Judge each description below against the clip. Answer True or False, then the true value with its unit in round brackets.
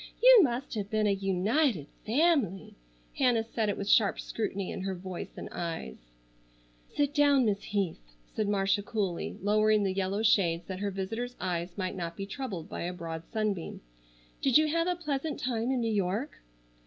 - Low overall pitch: False (205 Hz)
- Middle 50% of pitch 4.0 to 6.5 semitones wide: True (4.7 semitones)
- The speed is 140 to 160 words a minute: False (175 wpm)